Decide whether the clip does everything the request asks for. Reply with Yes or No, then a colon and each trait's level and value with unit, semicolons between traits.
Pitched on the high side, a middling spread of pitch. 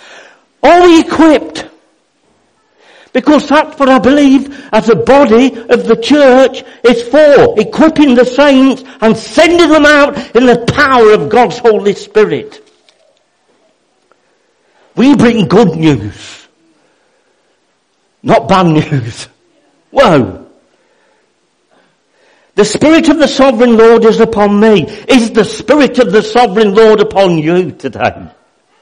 Yes: high, 240 Hz; average, 4.5 semitones